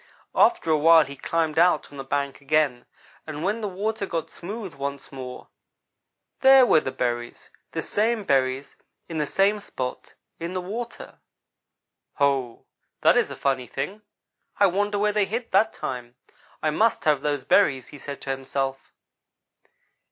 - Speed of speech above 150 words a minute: Yes, average, 160 wpm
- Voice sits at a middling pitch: Yes, medium, 155 Hz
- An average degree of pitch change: No, wide, 6.9 semitones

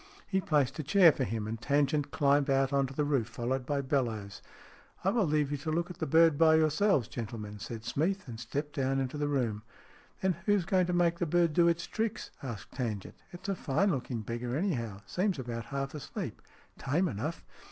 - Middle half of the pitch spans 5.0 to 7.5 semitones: Yes, wide, 5.6 semitones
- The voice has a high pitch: No, medium, 145 Hz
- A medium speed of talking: No, fast, 220 wpm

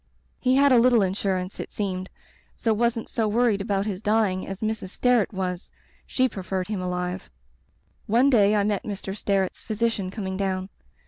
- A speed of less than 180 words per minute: Yes, average, 170 wpm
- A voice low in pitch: No, high, 205 Hz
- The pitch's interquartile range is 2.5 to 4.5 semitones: Yes, average, 3.1 semitones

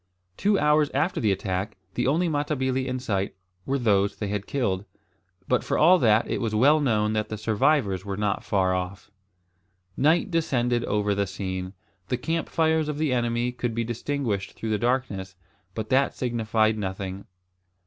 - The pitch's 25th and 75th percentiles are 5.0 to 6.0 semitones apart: Yes, wide, 5.5 semitones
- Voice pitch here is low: Yes, low, 115 Hz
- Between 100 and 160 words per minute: No, average, 170 wpm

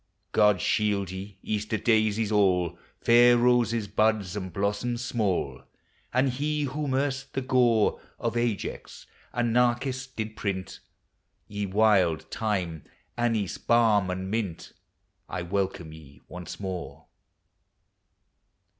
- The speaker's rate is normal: No, slow, 115 wpm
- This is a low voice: Yes, low, 110 Hz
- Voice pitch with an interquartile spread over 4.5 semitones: No, average, 3.9 semitones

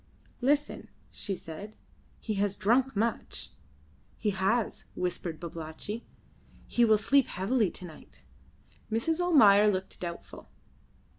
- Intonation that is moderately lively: Yes, average, 4.3 semitones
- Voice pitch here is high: Yes, high, 210 Hz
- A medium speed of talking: No, slow, 115 wpm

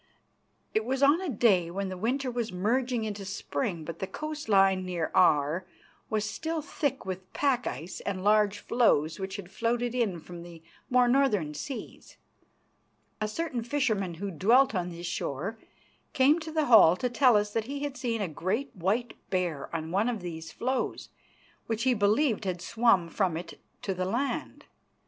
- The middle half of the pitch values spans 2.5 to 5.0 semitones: No, wide, 5.5 semitones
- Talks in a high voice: Yes, high, 210 Hz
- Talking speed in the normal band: Yes, average, 175 wpm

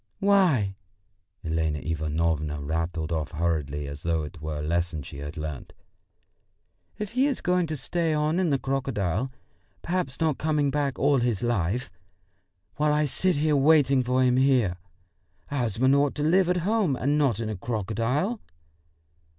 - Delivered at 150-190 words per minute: Yes, average, 160 wpm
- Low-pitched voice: Yes, low, 125 Hz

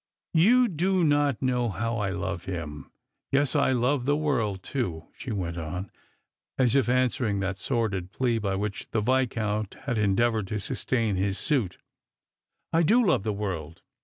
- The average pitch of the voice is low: Yes, low, 115 Hz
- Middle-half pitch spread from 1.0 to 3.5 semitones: No, average, 5.3 semitones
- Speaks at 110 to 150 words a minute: No, average, 170 wpm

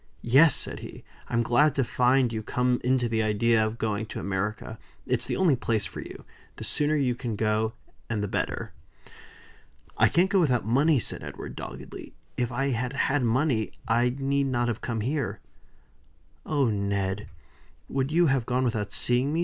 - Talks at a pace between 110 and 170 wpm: No, average, 180 wpm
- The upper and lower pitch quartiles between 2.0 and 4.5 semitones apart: Yes, average, 3.7 semitones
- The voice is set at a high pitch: No, low, 120 Hz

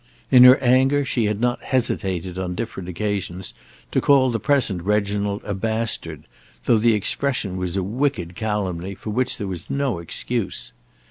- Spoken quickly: No, average, 160 wpm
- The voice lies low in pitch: Yes, low, 105 Hz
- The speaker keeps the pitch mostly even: No, average, 4.7 semitones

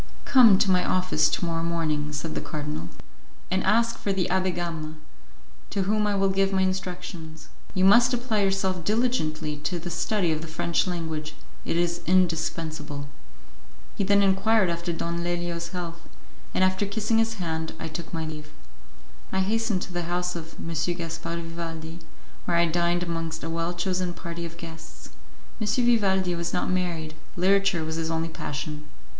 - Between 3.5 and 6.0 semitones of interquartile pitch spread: No, average, 2.7 semitones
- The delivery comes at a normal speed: Yes, average, 170 wpm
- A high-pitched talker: No, medium, 175 Hz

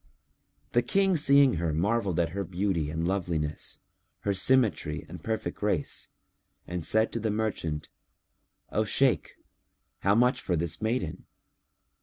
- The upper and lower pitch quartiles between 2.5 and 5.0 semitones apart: No, wide, 5.5 semitones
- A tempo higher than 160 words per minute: No, slow, 135 wpm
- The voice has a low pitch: Yes, low, 100 Hz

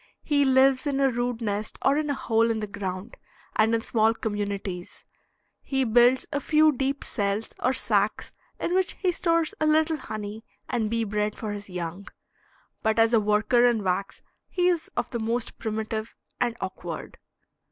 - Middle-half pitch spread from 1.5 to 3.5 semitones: No, average, 4.3 semitones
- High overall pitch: Yes, high, 225 Hz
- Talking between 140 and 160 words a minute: No, average, 175 wpm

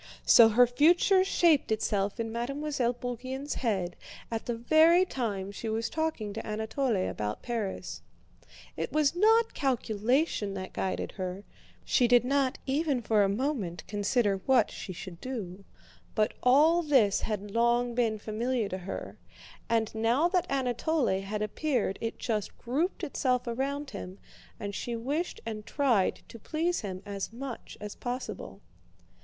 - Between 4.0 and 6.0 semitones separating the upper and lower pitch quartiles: Yes, average, 4.9 semitones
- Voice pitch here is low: No, high, 235 Hz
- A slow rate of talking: No, average, 150 wpm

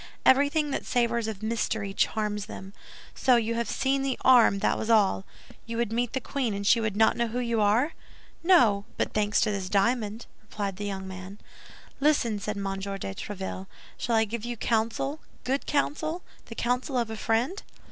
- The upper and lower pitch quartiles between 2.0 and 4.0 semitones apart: Yes, average, 3.4 semitones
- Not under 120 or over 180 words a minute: No, average, 190 wpm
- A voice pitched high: Yes, high, 225 Hz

